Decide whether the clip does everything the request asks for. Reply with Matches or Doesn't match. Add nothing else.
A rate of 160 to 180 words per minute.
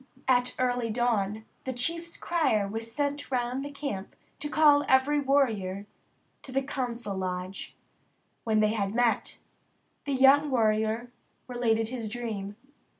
Doesn't match